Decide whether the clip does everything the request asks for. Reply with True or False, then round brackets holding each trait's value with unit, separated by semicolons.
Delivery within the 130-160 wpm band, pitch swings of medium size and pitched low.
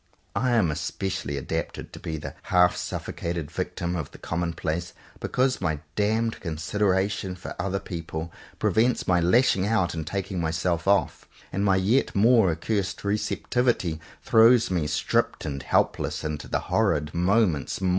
True (150 wpm; 3.9 semitones; 90 Hz)